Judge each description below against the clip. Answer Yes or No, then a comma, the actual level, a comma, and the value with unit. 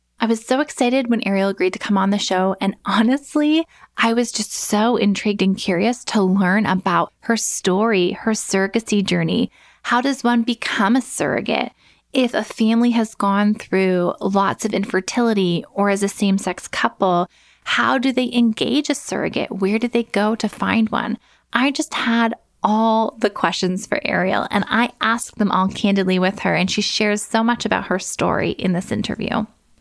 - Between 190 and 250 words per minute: No, average, 180 wpm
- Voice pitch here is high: Yes, high, 215 Hz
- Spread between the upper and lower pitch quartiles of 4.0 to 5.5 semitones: No, average, 3.3 semitones